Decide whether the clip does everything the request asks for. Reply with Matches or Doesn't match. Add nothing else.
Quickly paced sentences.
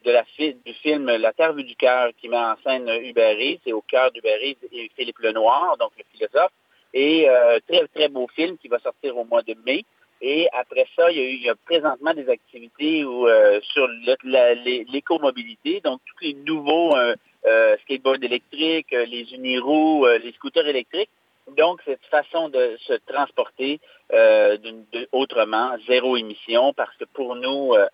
Doesn't match